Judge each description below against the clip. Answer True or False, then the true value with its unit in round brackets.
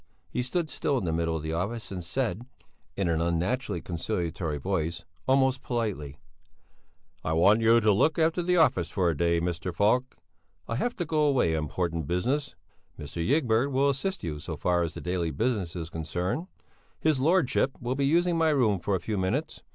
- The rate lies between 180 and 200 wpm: True (190 wpm)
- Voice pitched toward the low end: True (105 Hz)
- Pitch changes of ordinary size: False (8.1 semitones)